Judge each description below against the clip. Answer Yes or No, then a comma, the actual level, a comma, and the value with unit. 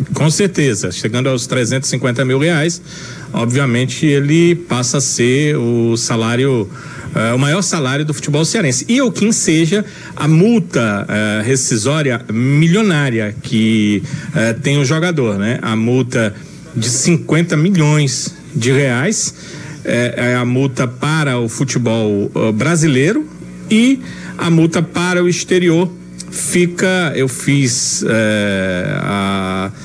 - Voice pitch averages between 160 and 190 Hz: No, medium, 140 Hz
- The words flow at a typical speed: Yes, average, 130 wpm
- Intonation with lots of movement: Yes, wide, 5.9 semitones